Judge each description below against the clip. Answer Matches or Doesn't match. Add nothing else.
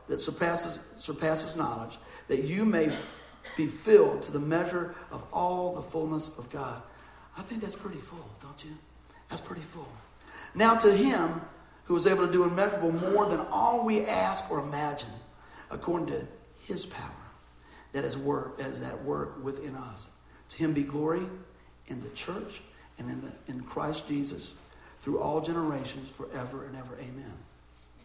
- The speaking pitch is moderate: Matches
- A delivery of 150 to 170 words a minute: Matches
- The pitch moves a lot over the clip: Matches